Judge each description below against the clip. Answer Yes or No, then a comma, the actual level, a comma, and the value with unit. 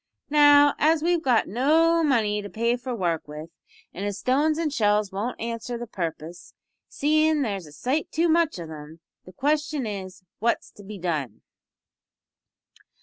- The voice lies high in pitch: Yes, high, 235 Hz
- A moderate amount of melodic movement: No, wide, 7.9 semitones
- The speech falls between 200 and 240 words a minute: No, average, 160 wpm